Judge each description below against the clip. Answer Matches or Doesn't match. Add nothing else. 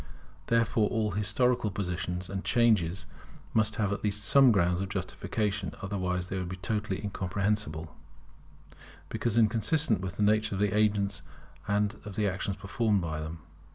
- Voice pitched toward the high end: Doesn't match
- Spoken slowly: Doesn't match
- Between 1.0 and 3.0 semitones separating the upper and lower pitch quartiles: Matches